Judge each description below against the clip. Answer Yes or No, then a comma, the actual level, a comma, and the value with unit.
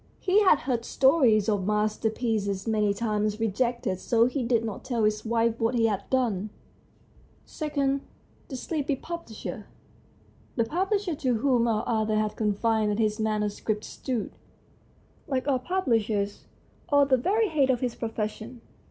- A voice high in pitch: Yes, high, 230 Hz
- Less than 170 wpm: Yes, average, 145 wpm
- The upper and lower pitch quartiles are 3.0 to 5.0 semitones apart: Yes, average, 3.8 semitones